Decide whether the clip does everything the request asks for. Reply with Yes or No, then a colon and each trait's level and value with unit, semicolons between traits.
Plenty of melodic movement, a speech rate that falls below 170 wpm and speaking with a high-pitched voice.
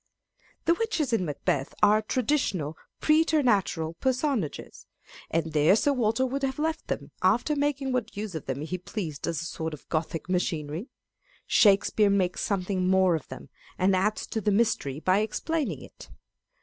Yes: wide, 7.6 semitones; average, 160 wpm; high, 200 Hz